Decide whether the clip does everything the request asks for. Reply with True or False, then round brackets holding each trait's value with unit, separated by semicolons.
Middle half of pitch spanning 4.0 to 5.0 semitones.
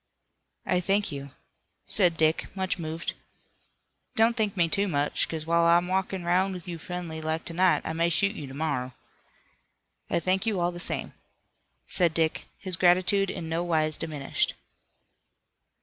False (2.7 semitones)